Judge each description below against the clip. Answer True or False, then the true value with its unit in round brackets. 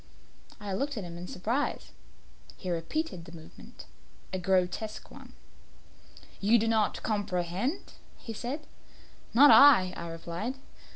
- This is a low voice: False (205 Hz)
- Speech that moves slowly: True (125 wpm)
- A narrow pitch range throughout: False (5.1 semitones)